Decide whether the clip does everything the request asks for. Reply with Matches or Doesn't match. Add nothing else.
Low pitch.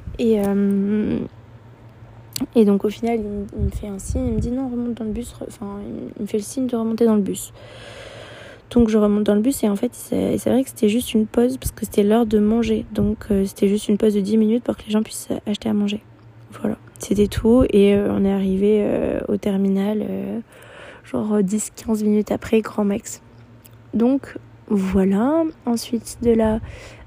Doesn't match